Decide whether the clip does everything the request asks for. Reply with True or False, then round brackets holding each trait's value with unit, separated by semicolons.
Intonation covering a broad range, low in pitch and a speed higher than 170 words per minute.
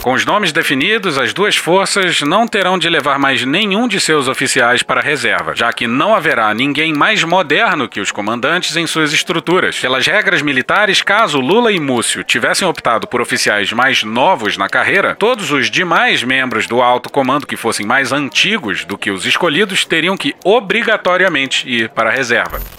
False (6.1 semitones; 165 Hz; 180 wpm)